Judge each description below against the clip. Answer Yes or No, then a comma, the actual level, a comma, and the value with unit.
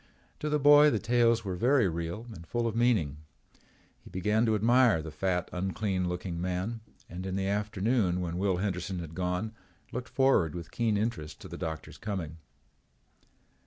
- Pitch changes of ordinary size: Yes, average, 4.5 semitones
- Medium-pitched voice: No, very low, 95 Hz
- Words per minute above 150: Yes, average, 170 wpm